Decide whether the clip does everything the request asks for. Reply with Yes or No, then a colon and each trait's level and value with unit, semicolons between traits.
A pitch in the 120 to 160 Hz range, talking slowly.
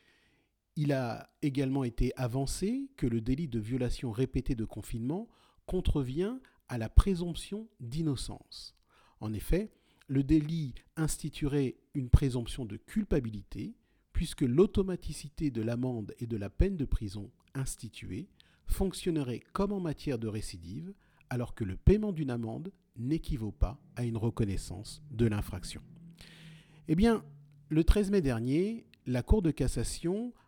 Yes: medium, 140 Hz; slow, 135 wpm